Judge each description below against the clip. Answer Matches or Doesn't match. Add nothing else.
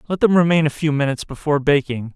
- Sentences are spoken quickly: Matches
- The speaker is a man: Matches